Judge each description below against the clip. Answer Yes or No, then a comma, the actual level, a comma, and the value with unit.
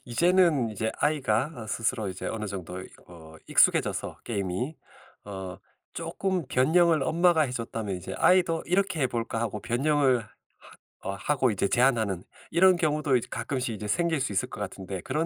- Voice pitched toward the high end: No, low, 125 Hz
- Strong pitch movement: Yes, wide, 7.5 semitones